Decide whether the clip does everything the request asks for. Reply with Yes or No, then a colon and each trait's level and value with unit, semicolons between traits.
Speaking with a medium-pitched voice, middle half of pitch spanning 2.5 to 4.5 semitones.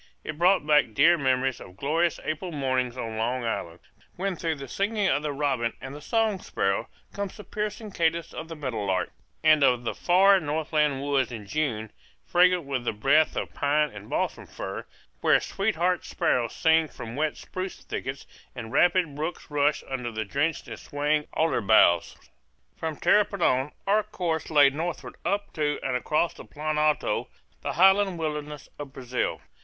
No: medium, 150 Hz; average, 4.9 semitones